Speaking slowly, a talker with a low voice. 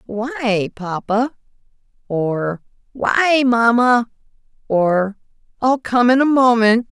No: slow, 95 wpm; high, 230 Hz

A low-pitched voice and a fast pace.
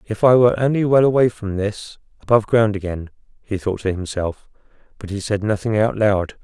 No: low, 105 Hz; average, 195 wpm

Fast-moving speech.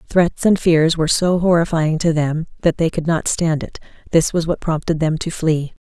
Yes: fast, 215 wpm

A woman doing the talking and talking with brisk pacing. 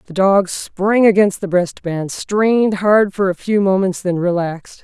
No: female; average, 185 wpm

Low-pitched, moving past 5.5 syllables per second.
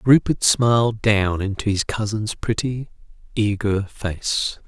No: low, 105 Hz; 3.7 syllables/s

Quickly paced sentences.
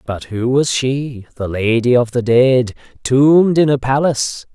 No: average, 170 wpm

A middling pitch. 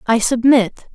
No: high, 235 Hz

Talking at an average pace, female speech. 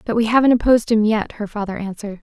No: fast, 235 wpm; female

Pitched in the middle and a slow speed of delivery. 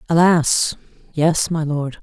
Yes: medium, 160 Hz; slow, 120 wpm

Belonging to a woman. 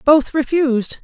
Yes: female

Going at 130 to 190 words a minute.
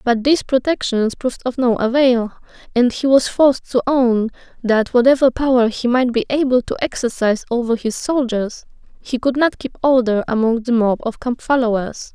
Yes: average, 175 wpm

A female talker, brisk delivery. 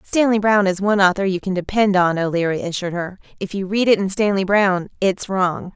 Yes: female; fast, 220 wpm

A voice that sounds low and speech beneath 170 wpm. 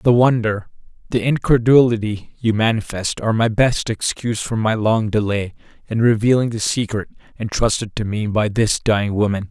Yes: low, 110 Hz; average, 160 wpm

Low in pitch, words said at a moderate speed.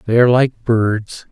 Yes: low, 115 Hz; average, 185 wpm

